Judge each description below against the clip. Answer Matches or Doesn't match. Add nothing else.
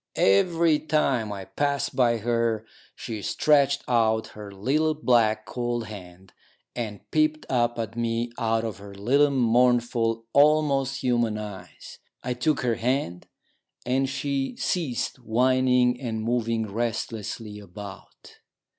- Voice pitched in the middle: Doesn't match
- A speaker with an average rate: Doesn't match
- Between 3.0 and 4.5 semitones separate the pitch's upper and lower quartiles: Matches